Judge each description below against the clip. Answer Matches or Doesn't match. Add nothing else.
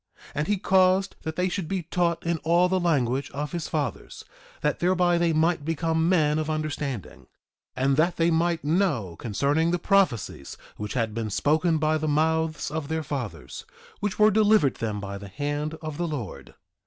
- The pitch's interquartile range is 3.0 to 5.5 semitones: Matches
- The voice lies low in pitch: Doesn't match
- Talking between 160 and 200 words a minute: Matches